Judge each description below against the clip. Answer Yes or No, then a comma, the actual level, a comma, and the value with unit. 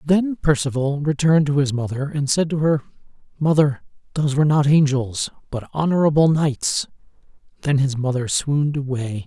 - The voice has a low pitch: No, medium, 145 Hz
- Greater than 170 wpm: No, average, 150 wpm